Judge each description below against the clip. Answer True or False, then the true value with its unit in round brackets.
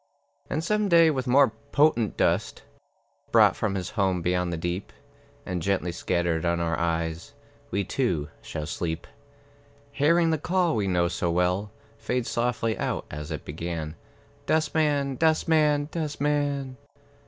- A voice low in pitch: True (105 Hz)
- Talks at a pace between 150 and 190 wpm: False (140 wpm)